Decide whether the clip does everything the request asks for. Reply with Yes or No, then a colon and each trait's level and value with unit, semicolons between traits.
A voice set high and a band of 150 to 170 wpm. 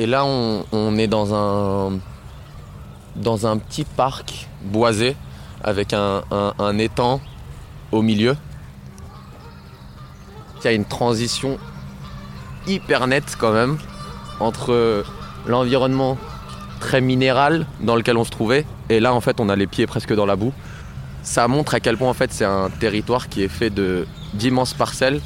No: low, 110 Hz; average, 155 wpm